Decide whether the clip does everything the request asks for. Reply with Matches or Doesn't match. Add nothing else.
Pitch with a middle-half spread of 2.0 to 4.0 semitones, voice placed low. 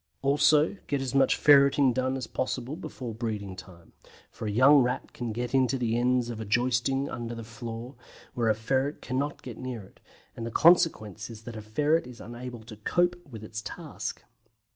Matches